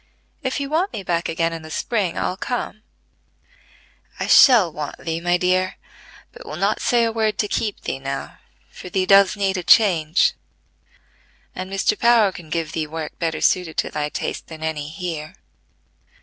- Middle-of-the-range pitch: Yes, medium, 180 Hz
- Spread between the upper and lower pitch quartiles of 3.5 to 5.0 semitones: Yes, average, 4.5 semitones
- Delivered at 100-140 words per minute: No, average, 175 wpm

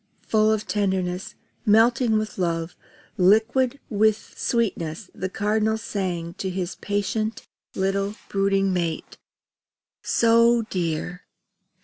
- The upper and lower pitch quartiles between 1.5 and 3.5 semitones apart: Yes, average, 3.1 semitones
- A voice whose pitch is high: Yes, high, 200 Hz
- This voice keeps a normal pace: No, slow, 100 wpm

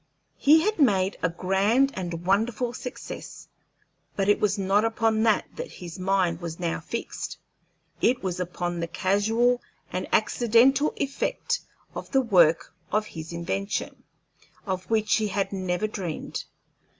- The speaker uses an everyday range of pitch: Yes, average, 4.3 semitones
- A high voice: Yes, high, 200 Hz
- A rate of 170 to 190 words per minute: No, average, 140 wpm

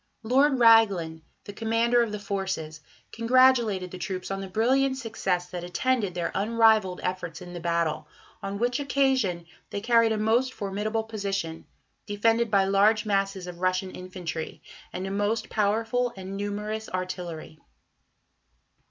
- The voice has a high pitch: Yes, high, 200 Hz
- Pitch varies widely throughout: No, average, 3.7 semitones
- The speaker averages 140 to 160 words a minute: Yes, average, 145 wpm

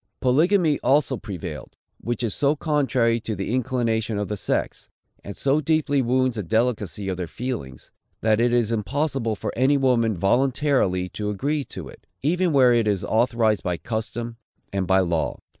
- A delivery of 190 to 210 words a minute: No, average, 170 wpm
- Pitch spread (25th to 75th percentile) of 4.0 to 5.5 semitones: Yes, average, 4.5 semitones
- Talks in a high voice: No, low, 115 Hz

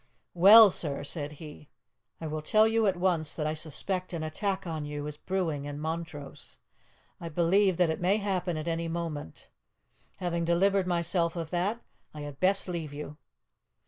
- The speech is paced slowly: No, average, 175 wpm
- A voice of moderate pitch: Yes, medium, 170 Hz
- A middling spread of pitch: Yes, average, 3.4 semitones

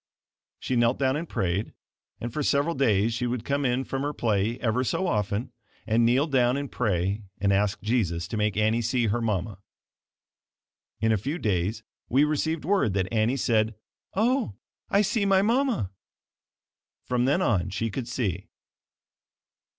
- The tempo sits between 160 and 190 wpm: Yes, average, 165 wpm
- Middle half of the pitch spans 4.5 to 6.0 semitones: Yes, average, 5.0 semitones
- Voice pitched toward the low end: Yes, low, 120 Hz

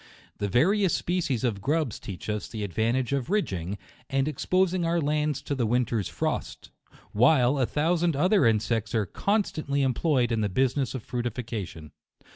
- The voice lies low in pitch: Yes, low, 130 Hz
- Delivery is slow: No, average, 165 wpm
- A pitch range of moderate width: No, wide, 5.7 semitones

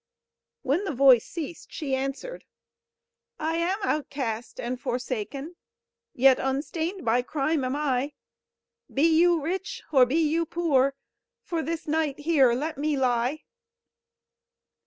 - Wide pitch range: No, average, 3.8 semitones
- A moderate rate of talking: No, slow, 125 wpm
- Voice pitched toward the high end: Yes, very high, 290 Hz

